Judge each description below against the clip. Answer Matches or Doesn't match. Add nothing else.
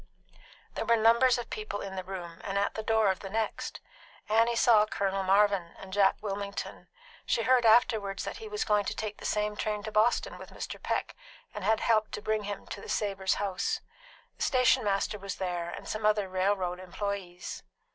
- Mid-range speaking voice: Doesn't match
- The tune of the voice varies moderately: Doesn't match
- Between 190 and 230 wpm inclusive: Matches